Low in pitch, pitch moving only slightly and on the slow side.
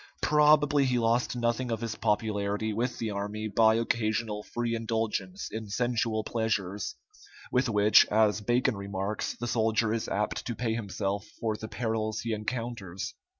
No: low, 110 Hz; narrow, 2.1 semitones; average, 150 wpm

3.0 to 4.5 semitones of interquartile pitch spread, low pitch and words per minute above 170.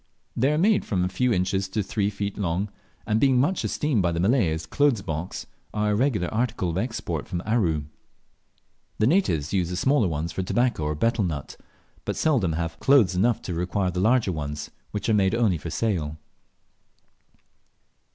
No: wide, 5.6 semitones; very low, 95 Hz; average, 190 wpm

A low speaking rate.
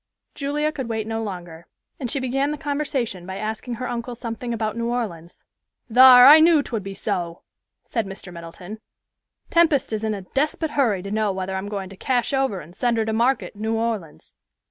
No: average, 200 wpm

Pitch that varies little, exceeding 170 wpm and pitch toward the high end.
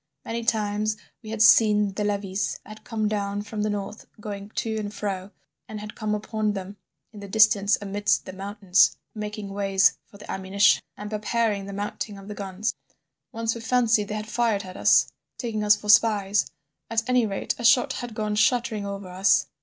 Yes: narrow, 1.5 semitones; average, 190 wpm; high, 210 Hz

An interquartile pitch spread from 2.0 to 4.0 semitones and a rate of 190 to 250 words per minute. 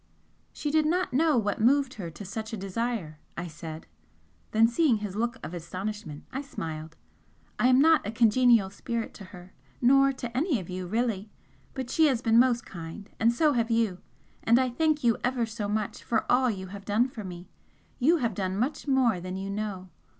No: average, 4.9 semitones; average, 200 wpm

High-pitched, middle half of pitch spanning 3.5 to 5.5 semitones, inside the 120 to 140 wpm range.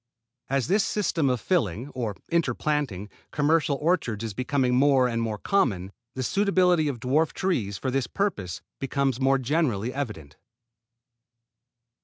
No: low, 135 Hz; average, 5.2 semitones; slow, 135 wpm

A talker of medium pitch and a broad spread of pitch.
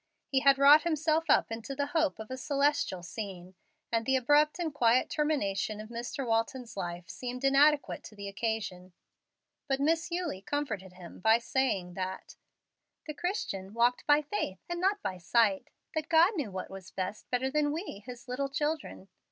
No: very high, 255 Hz; wide, 6.7 semitones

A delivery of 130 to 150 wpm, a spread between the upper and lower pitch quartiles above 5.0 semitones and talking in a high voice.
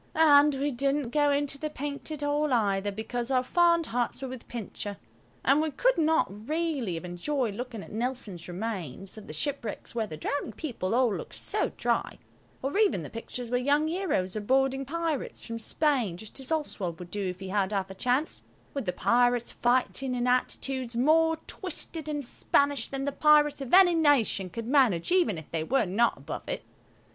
No: average, 190 wpm; wide, 5.6 semitones; very high, 255 Hz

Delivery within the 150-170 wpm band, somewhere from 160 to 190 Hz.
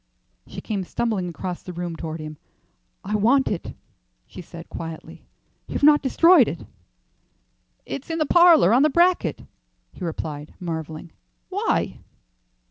No: slow, 135 wpm; medium, 185 Hz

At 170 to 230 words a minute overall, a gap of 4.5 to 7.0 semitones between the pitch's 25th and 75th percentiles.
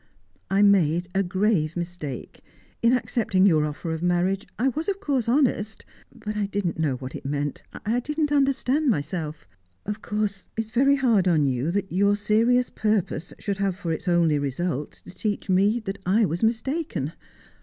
Yes: average, 175 wpm; average, 5.1 semitones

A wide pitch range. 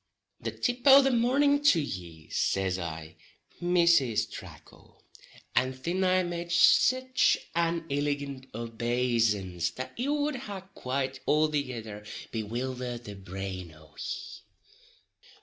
Yes: wide, 8.8 semitones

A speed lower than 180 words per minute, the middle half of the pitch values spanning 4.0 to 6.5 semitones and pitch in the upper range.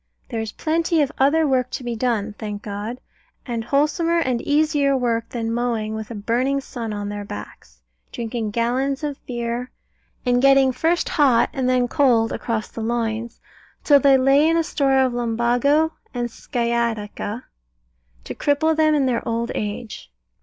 No: average, 165 wpm; average, 3.4 semitones; high, 245 Hz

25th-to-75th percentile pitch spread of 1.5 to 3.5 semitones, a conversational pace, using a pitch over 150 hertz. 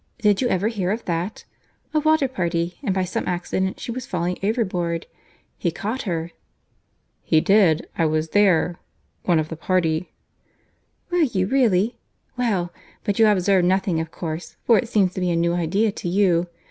No: average, 4.0 semitones; average, 160 wpm; medium, 185 Hz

